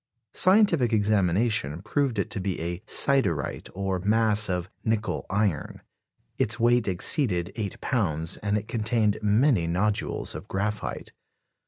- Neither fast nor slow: No, slow, 130 wpm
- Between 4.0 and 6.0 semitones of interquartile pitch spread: No, average, 3.5 semitones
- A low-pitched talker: Yes, low, 105 Hz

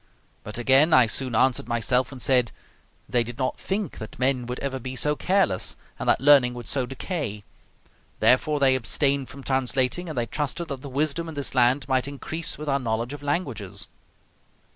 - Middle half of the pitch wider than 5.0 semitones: No, average, 2.8 semitones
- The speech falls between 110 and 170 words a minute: No, average, 185 wpm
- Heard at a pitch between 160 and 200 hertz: No, low, 130 Hz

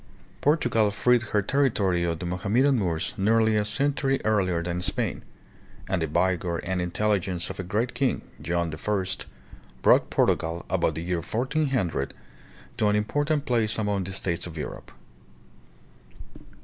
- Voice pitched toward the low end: Yes, low, 100 Hz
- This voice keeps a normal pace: Yes, average, 145 wpm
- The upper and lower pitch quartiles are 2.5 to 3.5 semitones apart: No, average, 4.8 semitones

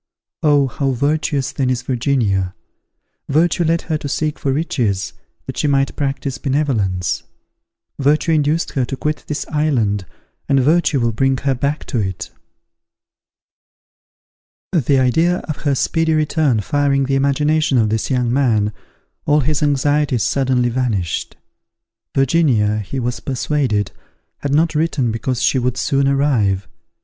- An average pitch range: Yes, average, 3.5 semitones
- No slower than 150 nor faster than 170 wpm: No, average, 140 wpm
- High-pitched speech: No, low, 135 Hz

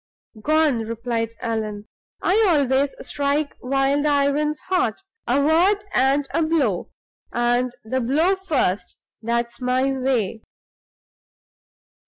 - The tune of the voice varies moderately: Yes, average, 4.2 semitones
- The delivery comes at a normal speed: No, slow, 110 wpm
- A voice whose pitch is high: Yes, very high, 270 Hz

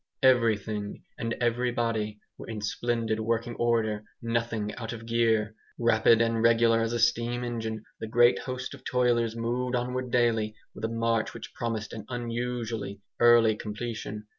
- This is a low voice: Yes, low, 115 Hz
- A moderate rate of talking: Yes, average, 150 wpm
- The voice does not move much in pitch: Yes, narrow, 1.3 semitones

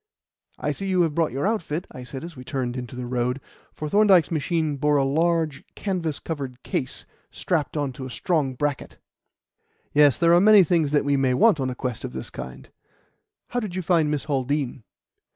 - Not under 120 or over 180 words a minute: No, average, 200 wpm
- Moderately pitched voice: Yes, medium, 150 Hz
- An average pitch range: Yes, average, 4.4 semitones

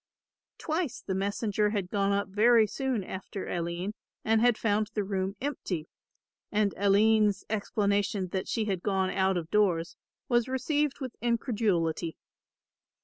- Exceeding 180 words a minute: No, average, 140 wpm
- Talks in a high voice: Yes, high, 205 Hz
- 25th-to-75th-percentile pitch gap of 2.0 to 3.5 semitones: Yes, average, 2.9 semitones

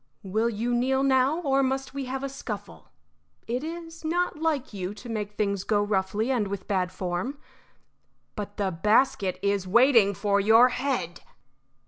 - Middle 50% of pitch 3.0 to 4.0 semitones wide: No, average, 5.0 semitones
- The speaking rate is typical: Yes, average, 160 wpm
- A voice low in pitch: No, high, 225 Hz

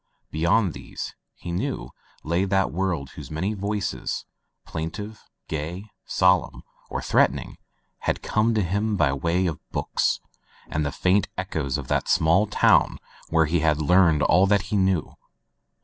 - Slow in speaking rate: No, average, 150 wpm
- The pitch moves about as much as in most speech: Yes, average, 3.8 semitones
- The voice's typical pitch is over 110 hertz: No, very low, 90 Hz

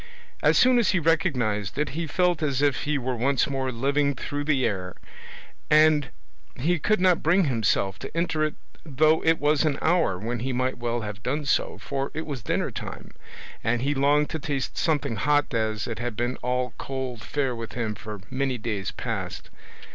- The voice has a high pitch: No, low, 135 Hz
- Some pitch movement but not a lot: Yes, average, 4.3 semitones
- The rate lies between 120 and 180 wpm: No, average, 195 wpm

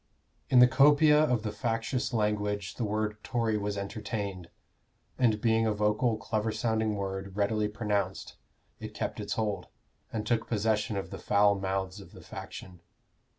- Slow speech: No, average, 155 wpm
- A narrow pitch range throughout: Yes, narrow, 1.9 semitones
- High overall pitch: No, low, 105 Hz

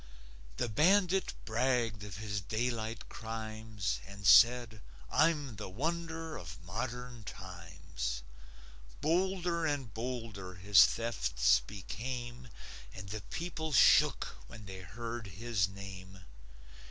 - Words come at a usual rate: No, slow, 105 wpm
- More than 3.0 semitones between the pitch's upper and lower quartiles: Yes, average, 4.6 semitones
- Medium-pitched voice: No, low, 115 Hz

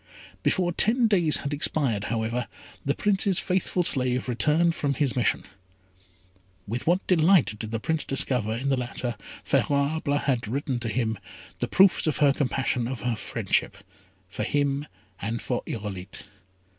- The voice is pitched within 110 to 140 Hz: Yes, low, 135 Hz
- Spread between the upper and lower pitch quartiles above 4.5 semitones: Yes, average, 5.1 semitones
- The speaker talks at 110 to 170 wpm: Yes, average, 155 wpm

